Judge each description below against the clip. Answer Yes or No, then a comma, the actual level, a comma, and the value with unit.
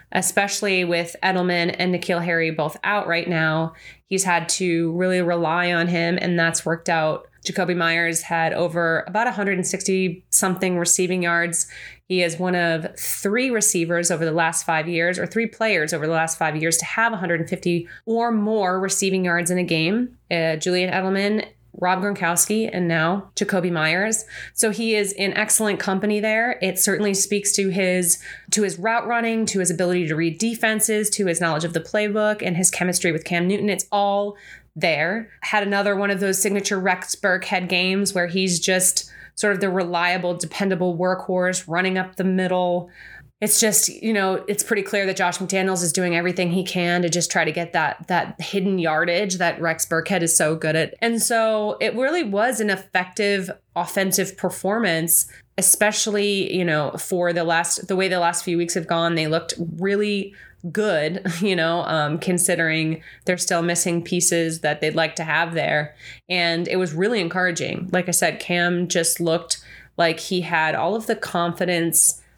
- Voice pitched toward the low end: No, medium, 180 Hz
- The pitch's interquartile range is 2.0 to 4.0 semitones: Yes, average, 2.8 semitones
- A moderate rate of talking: Yes, average, 180 wpm